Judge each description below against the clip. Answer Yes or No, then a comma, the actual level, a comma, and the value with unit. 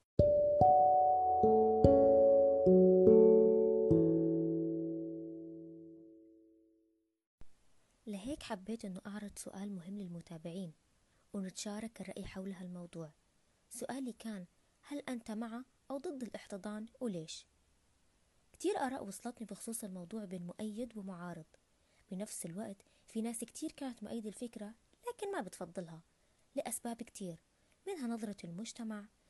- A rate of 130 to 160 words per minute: No, average, 90 wpm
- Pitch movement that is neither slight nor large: No, wide, 8.2 semitones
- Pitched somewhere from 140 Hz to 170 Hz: No, high, 190 Hz